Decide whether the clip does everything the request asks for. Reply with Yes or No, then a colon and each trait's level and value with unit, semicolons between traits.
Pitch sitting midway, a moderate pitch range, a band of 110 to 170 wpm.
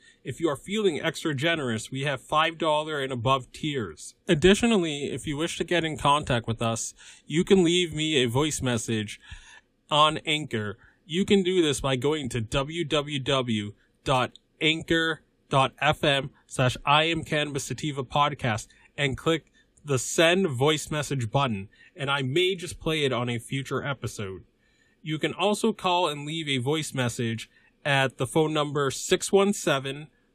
Yes: medium, 145 Hz; average, 4.1 semitones; average, 140 wpm